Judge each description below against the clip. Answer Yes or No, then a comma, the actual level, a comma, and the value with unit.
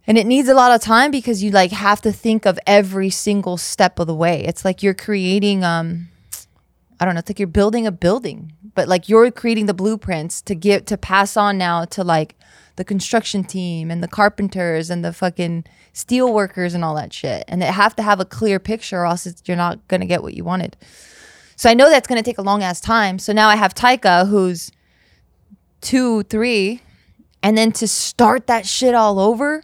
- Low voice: No, high, 200 Hz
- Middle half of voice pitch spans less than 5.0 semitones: Yes, average, 3.7 semitones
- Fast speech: Yes, fast, 220 wpm